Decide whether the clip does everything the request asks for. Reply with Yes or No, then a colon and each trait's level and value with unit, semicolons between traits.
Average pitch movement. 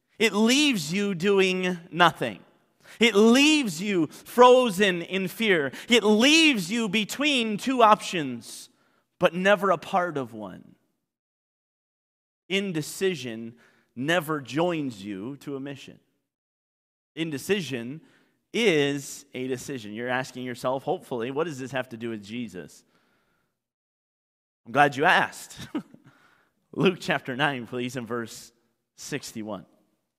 No: wide, 8.3 semitones